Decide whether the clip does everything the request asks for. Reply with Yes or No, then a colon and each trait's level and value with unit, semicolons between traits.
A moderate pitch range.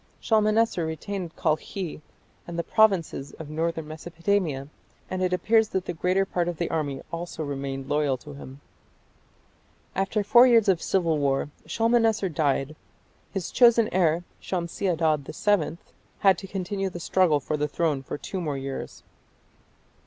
Yes: average, 4.3 semitones